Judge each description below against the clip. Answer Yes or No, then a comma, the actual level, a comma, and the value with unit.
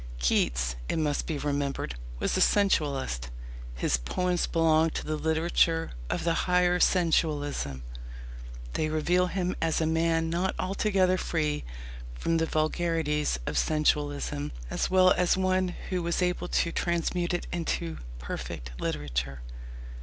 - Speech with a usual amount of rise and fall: Yes, average, 3.4 semitones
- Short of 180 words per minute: Yes, slow, 135 wpm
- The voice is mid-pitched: Yes, medium, 160 Hz